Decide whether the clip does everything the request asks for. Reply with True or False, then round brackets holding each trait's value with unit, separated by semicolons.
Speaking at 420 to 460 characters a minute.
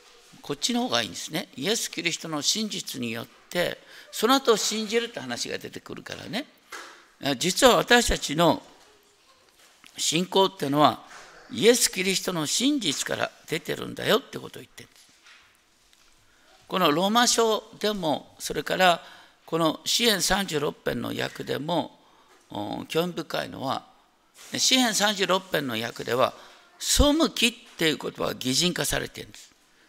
False (275 characters per minute)